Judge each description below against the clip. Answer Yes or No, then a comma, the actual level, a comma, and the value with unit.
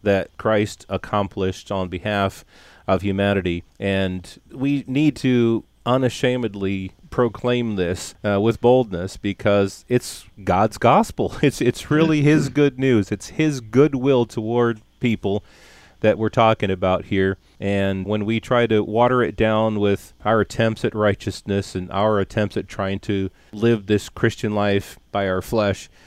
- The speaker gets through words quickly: No, average, 145 wpm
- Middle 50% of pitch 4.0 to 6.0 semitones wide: No, average, 3.5 semitones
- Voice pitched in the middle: No, low, 105 Hz